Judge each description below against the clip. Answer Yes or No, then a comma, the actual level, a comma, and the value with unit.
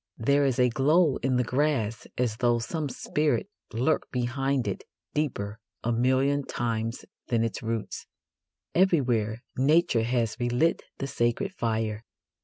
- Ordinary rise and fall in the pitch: Yes, average, 3.7 semitones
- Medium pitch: No, low, 125 Hz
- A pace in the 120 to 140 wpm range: Yes, slow, 135 wpm